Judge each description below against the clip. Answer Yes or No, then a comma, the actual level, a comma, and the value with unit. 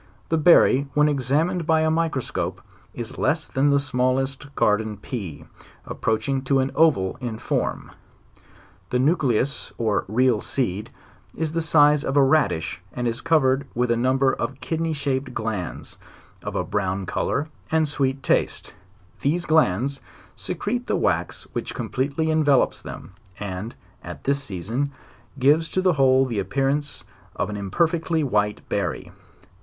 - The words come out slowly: No, average, 150 wpm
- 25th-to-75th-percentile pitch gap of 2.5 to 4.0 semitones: No, average, 4.6 semitones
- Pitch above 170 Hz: No, low, 135 Hz